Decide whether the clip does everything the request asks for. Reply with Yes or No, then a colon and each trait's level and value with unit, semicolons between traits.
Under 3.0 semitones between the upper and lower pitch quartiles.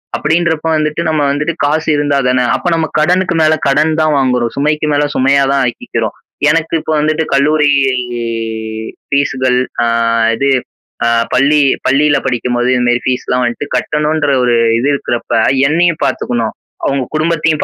No: average, 3.3 semitones